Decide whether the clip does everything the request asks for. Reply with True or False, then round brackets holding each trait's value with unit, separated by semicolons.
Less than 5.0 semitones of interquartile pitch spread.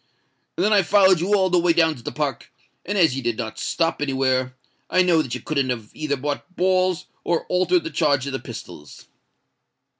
False (5.6 semitones)